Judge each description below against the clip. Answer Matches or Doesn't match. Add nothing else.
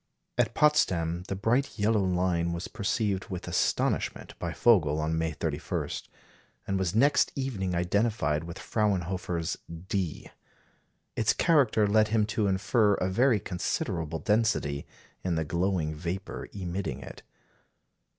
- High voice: Doesn't match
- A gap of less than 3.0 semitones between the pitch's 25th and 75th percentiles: Doesn't match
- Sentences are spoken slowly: Matches